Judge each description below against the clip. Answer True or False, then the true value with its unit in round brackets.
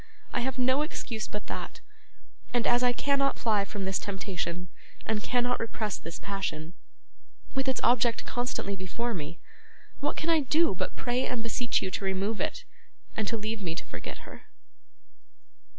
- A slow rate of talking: False (165 wpm)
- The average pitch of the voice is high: True (225 Hz)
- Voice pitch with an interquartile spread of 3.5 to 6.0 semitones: True (4.3 semitones)